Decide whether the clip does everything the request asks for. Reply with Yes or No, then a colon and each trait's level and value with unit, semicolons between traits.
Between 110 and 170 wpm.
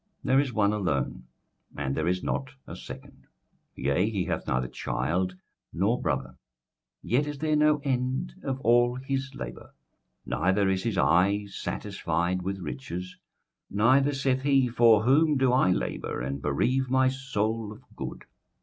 Yes: average, 155 wpm